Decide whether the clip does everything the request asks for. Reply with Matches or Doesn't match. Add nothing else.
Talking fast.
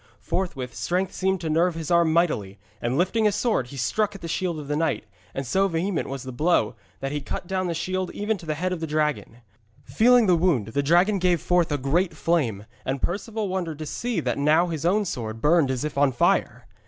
Matches